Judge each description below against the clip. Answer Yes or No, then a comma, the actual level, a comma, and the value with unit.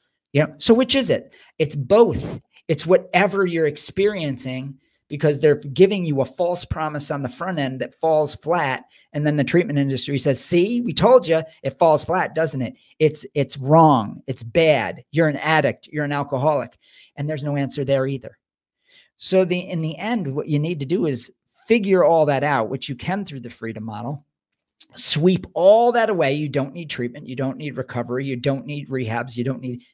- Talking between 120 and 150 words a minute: No, average, 200 wpm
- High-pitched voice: No, medium, 150 Hz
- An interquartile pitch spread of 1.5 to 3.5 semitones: No, average, 4.3 semitones